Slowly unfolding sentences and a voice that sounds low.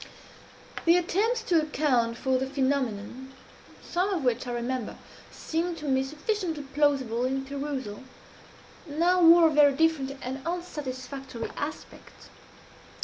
No: slow, 125 wpm; very high, 280 Hz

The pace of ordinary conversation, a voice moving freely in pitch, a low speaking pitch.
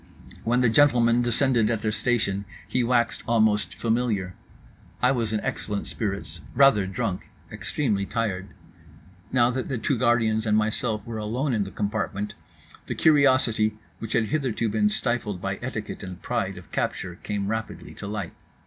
No: average, 160 wpm; average, 2.7 semitones; low, 110 Hz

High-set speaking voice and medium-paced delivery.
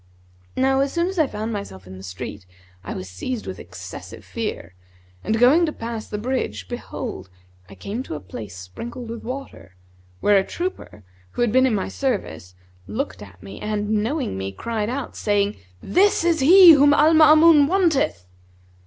Yes: high, 215 Hz; average, 175 wpm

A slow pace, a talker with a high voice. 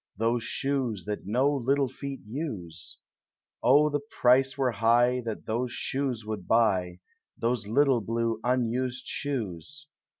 No: slow, 130 wpm; low, 120 Hz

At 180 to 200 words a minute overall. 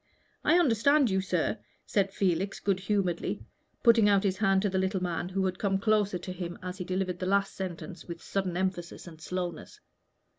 Yes: average, 190 wpm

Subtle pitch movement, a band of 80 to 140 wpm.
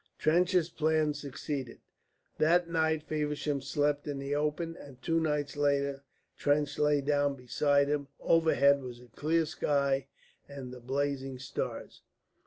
Yes: narrow, 1.8 semitones; slow, 135 wpm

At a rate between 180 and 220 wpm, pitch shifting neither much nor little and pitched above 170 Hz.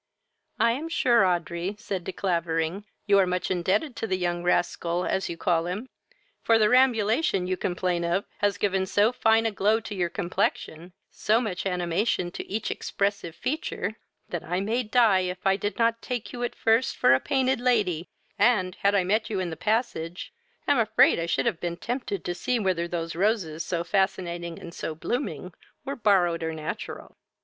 Yes: average, 190 wpm; average, 4.3 semitones; high, 190 Hz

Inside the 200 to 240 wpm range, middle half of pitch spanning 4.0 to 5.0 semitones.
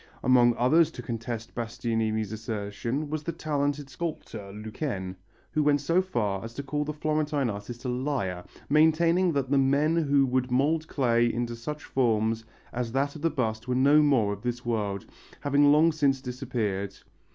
No: average, 170 wpm; average, 4.6 semitones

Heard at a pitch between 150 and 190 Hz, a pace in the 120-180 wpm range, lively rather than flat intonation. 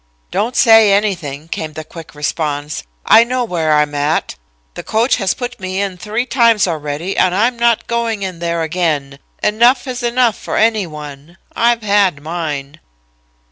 Yes: medium, 185 Hz; average, 170 wpm; wide, 6.7 semitones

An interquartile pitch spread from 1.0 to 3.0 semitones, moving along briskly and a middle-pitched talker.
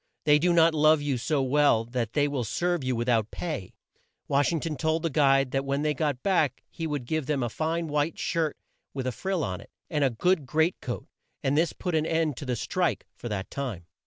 No: average, 3.8 semitones; fast, 235 wpm; medium, 145 Hz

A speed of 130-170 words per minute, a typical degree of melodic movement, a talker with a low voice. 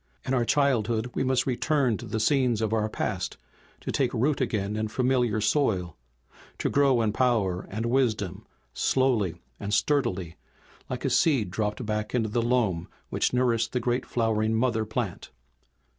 Yes: average, 160 wpm; average, 3.0 semitones; low, 115 Hz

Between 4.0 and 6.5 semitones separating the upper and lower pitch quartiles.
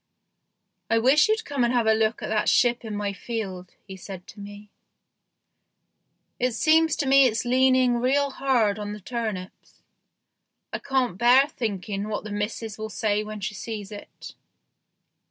No: average, 3.6 semitones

